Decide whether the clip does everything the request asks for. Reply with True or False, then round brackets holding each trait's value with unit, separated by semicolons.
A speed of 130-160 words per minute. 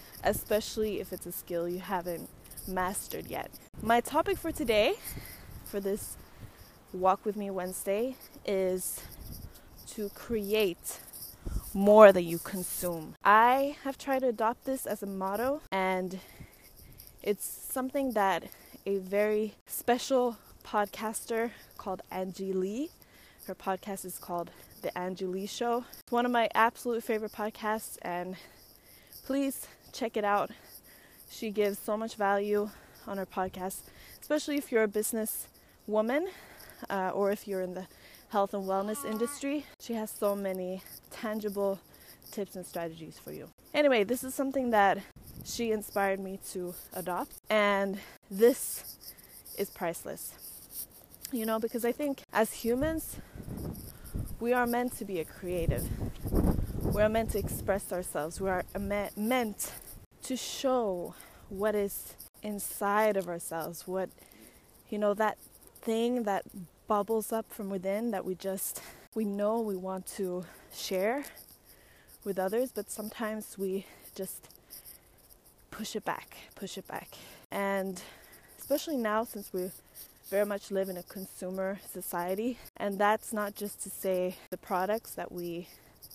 True (140 wpm)